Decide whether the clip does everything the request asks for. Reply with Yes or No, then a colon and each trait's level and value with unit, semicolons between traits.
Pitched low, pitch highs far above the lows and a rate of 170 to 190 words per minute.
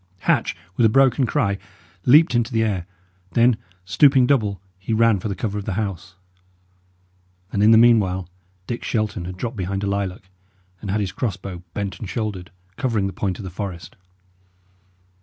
No: low, 105 Hz; average, 3.4 semitones; average, 175 wpm